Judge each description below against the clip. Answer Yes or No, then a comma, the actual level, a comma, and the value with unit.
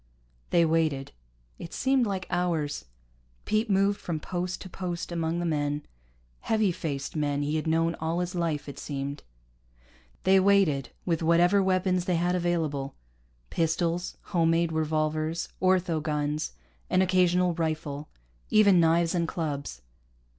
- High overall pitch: No, medium, 170 Hz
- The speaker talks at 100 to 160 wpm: Yes, average, 140 wpm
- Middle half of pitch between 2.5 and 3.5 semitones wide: Yes, average, 2.8 semitones